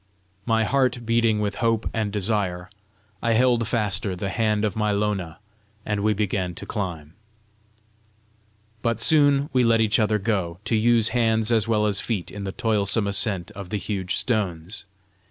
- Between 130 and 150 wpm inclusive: No, average, 165 wpm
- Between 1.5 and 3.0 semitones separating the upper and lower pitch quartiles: Yes, narrow, 2.6 semitones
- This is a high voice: No, low, 105 Hz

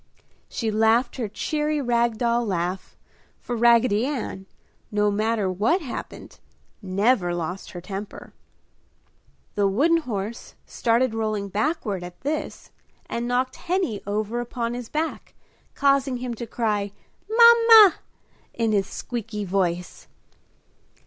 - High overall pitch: Yes, high, 230 Hz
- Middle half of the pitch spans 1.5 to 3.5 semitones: No, average, 3.9 semitones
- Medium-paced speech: No, slow, 120 wpm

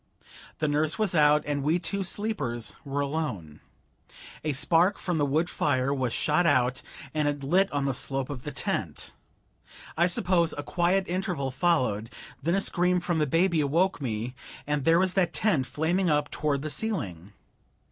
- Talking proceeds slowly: No, average, 175 wpm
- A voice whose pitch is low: No, medium, 150 Hz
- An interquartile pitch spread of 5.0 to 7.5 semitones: No, average, 4.3 semitones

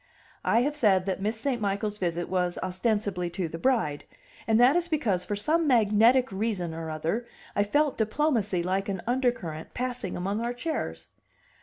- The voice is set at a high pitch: Yes, high, 210 Hz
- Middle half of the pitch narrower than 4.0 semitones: No, average, 5.1 semitones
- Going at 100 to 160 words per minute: No, average, 170 wpm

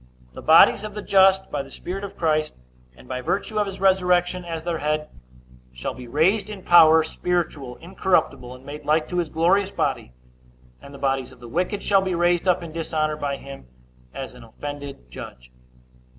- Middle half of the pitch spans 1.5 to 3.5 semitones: No, average, 4.8 semitones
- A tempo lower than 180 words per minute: No, average, 190 wpm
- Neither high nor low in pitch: Yes, medium, 160 Hz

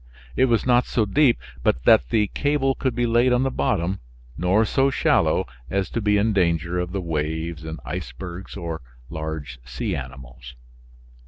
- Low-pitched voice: Yes, very low, 90 Hz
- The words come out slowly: No, average, 165 wpm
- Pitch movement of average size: No, wide, 7.0 semitones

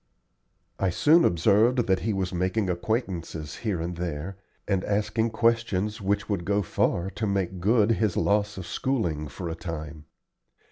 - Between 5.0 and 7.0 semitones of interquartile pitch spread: No, average, 3.7 semitones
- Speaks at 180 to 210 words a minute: No, average, 155 wpm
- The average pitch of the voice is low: Yes, low, 100 Hz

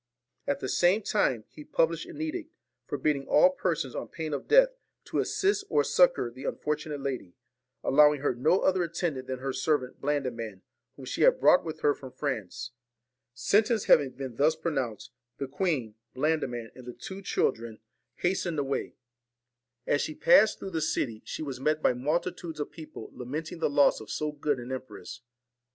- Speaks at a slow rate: No, average, 190 wpm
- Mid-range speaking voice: Yes, medium, 150 Hz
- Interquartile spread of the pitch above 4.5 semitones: Yes, average, 4.9 semitones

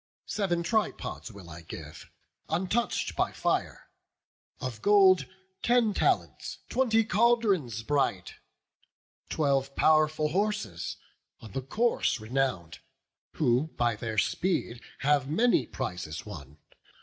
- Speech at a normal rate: No, slow, 105 wpm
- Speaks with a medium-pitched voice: Yes, medium, 145 Hz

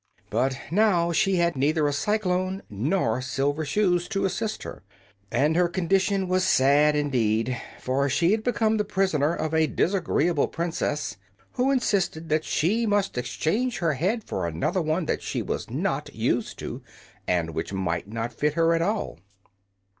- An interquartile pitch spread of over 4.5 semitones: Yes, wide, 5.5 semitones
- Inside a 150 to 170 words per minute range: Yes, average, 160 wpm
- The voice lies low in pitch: No, medium, 165 Hz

